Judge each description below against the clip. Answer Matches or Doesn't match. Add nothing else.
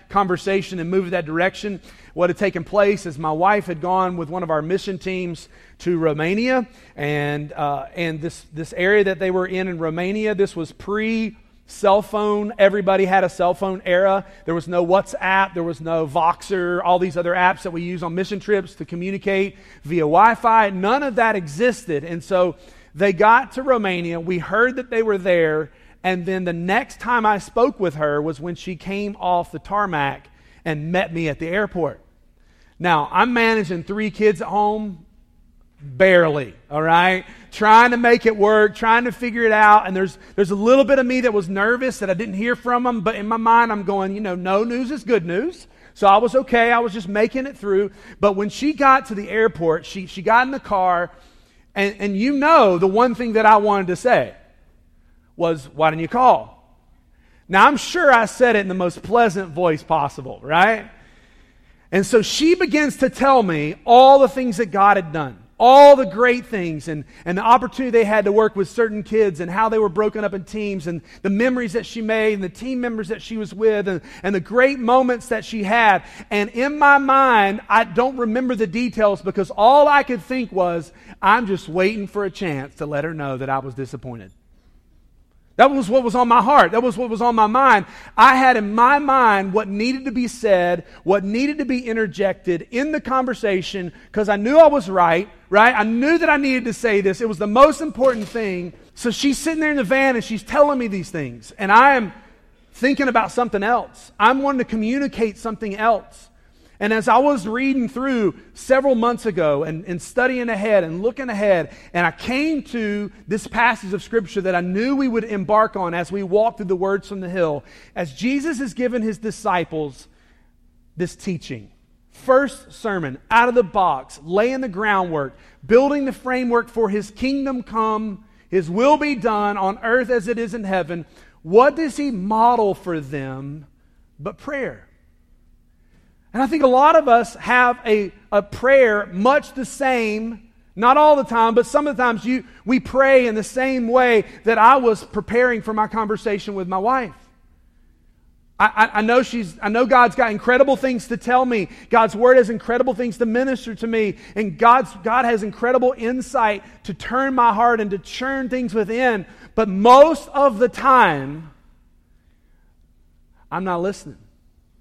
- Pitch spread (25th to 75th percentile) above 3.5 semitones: Matches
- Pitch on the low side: Doesn't match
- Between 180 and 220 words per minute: Matches